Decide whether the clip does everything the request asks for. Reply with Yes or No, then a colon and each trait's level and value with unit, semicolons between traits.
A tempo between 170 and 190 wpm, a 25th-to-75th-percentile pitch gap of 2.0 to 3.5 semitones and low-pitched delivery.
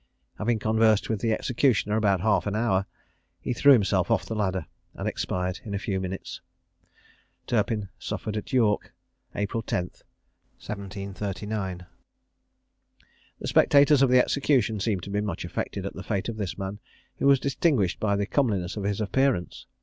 No: average, 160 wpm; average, 2.8 semitones; low, 105 Hz